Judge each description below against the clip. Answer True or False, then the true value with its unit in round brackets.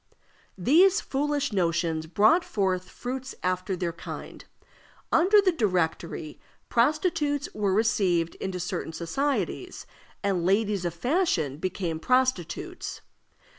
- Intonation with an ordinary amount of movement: False (8.5 semitones)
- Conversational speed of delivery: False (105 wpm)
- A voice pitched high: True (195 Hz)